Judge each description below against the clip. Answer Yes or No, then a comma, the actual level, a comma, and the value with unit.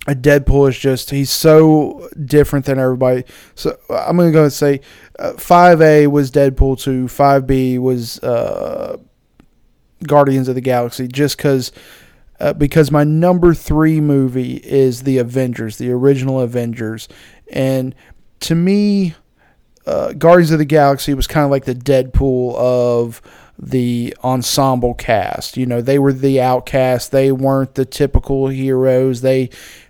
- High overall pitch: No, low, 135 Hz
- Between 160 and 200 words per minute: No, average, 145 wpm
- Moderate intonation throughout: No, narrow, 2.3 semitones